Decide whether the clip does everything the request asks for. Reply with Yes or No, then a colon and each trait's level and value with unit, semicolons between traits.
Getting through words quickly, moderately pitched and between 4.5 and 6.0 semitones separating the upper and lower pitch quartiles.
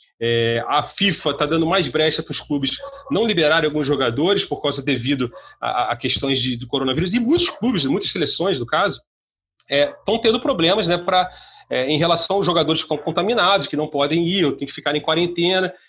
Yes: fast, 200 wpm; medium, 160 Hz; average, 5.0 semitones